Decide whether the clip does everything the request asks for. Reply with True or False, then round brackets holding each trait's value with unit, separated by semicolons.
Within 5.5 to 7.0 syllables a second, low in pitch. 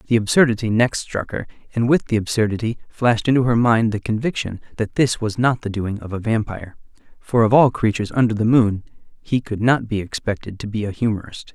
True (5.8 syllables/s; 115 Hz)